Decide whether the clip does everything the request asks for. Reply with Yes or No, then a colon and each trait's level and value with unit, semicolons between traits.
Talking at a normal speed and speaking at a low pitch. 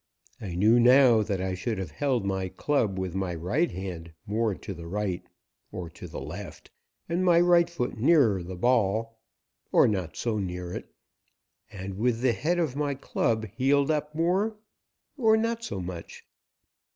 Yes: average, 170 wpm; low, 115 Hz